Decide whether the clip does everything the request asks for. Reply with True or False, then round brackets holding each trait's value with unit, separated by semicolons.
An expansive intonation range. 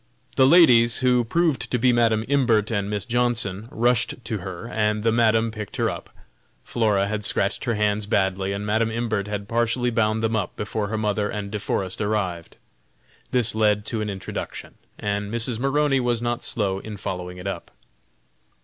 False (2.6 semitones)